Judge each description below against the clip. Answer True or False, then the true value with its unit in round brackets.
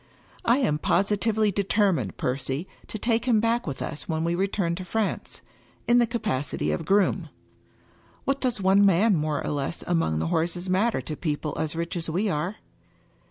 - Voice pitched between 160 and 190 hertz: True (185 Hz)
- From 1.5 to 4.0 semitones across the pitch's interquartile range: False (5.6 semitones)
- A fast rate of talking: False (180 wpm)